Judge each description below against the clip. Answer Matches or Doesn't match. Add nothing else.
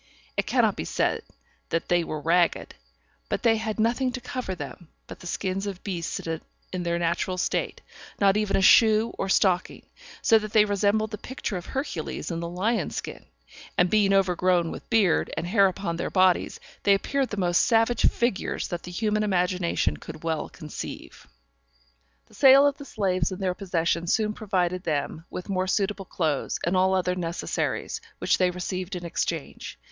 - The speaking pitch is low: Doesn't match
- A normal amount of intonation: Matches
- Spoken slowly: Doesn't match